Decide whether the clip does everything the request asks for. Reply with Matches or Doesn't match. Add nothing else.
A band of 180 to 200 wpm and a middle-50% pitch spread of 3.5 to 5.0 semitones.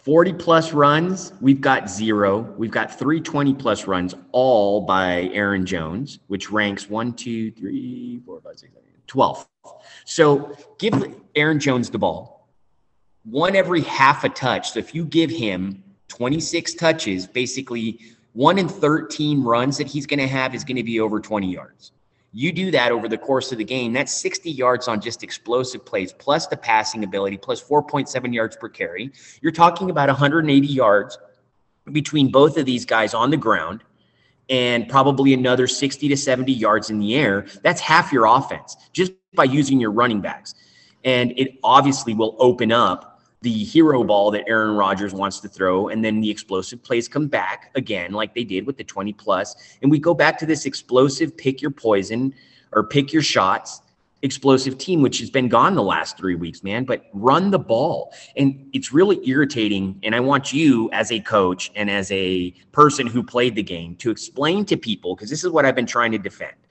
Doesn't match